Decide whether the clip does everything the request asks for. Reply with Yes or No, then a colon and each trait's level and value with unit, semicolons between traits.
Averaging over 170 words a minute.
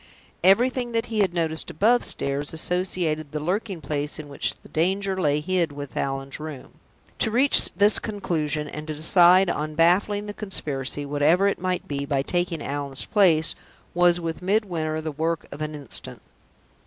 No: average, 165 wpm